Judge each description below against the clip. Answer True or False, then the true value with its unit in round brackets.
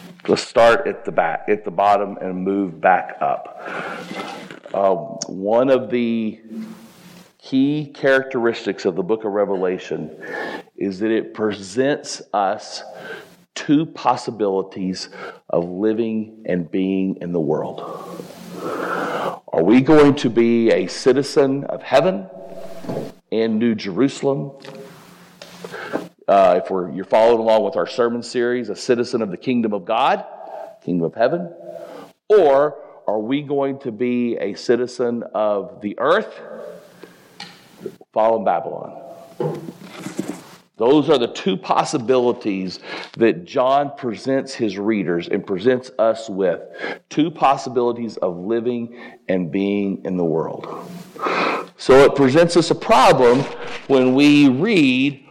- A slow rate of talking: True (125 wpm)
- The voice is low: True (120 Hz)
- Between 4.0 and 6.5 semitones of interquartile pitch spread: True (5.1 semitones)